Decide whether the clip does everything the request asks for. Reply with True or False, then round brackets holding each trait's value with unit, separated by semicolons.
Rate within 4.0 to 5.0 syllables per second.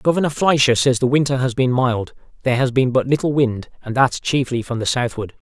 False (5.7 syllables/s)